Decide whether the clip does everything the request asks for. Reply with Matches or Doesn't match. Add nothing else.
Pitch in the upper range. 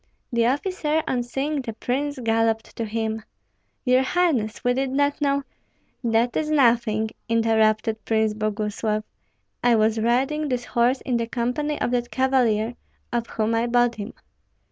Matches